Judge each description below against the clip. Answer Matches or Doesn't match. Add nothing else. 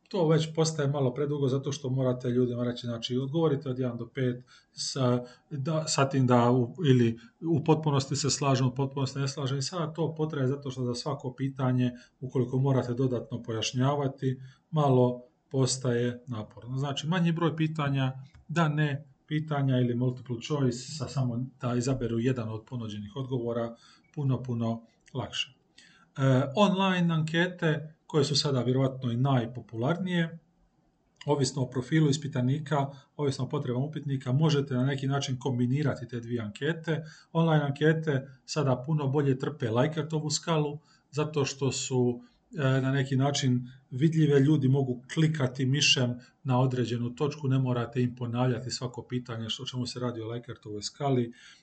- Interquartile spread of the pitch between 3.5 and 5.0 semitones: Doesn't match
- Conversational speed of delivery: Matches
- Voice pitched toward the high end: Doesn't match